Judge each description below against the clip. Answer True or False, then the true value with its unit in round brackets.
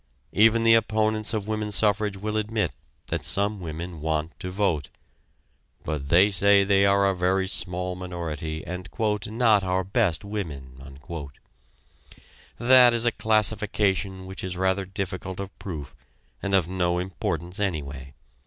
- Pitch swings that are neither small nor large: True (3.3 semitones)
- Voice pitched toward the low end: True (95 Hz)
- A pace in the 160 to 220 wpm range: False (140 wpm)